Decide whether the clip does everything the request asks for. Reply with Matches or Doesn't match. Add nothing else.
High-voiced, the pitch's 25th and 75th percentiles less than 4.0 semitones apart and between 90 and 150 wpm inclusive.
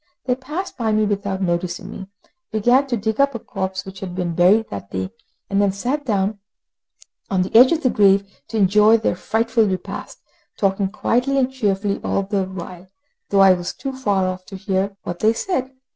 Doesn't match